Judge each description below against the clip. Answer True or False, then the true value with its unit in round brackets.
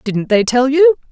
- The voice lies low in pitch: False (235 Hz)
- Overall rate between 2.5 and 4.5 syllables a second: True (4.4 syllables/s)